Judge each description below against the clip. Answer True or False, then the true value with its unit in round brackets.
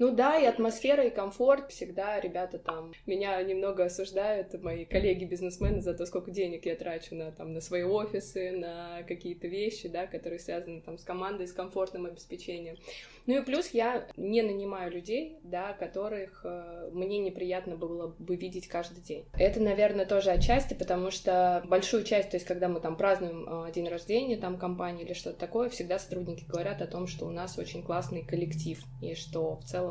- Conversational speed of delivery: False (180 wpm)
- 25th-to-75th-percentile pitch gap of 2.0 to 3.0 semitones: True (2.5 semitones)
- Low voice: False (180 Hz)